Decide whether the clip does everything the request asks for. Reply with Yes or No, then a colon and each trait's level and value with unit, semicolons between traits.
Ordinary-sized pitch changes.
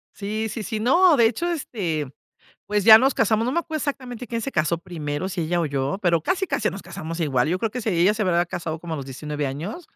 No: wide, 6.4 semitones